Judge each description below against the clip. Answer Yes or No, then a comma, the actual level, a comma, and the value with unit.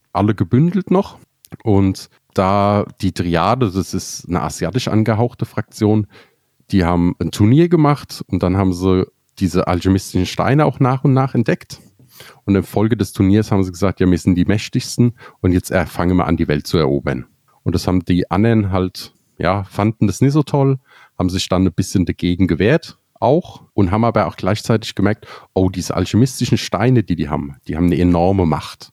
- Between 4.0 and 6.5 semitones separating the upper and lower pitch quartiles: Yes, average, 4.6 semitones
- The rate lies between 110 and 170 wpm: No, average, 185 wpm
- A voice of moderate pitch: No, low, 100 Hz